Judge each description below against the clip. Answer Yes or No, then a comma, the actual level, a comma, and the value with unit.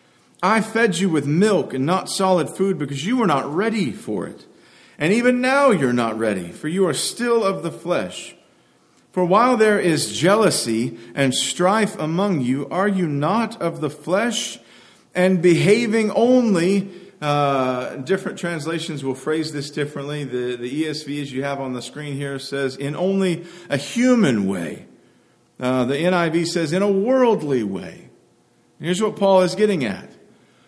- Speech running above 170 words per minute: No, average, 165 wpm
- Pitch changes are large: Yes, wide, 5.9 semitones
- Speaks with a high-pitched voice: No, medium, 175 Hz